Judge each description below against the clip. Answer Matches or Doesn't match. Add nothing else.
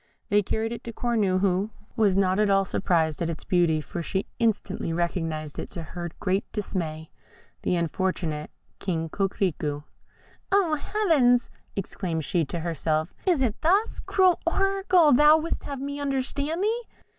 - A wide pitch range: Matches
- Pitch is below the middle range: Doesn't match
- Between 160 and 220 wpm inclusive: Doesn't match